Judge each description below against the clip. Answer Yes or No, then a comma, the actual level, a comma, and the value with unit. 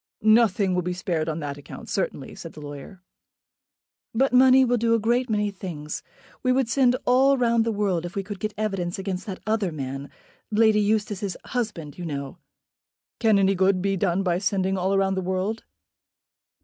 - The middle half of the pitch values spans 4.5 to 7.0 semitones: No, average, 3.8 semitones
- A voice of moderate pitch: No, high, 195 Hz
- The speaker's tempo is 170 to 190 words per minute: Yes, average, 185 wpm